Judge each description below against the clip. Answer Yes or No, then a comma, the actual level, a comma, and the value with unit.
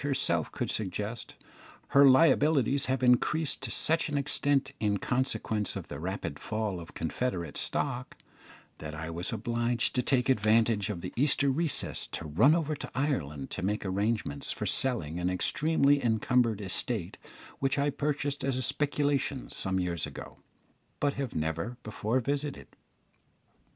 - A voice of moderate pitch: No, low, 120 Hz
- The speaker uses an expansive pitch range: Yes, wide, 6.7 semitones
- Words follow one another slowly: No, average, 150 wpm